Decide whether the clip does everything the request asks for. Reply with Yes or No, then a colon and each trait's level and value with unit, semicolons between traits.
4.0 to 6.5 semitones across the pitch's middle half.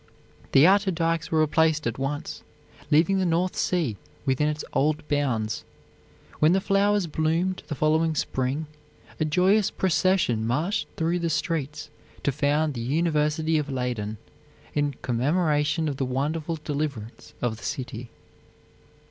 No: average, 3.5 semitones